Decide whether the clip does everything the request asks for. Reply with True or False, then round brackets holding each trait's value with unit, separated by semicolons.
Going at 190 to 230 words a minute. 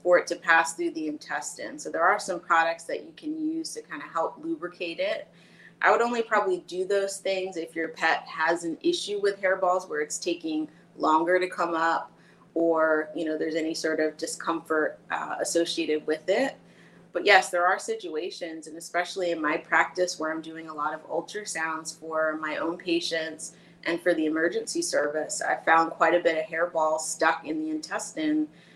True (195 wpm)